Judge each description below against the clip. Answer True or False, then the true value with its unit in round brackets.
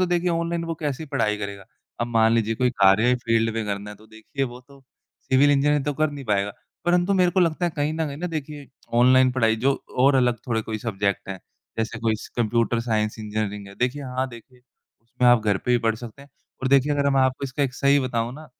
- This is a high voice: False (125 Hz)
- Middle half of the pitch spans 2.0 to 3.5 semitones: False (4.2 semitones)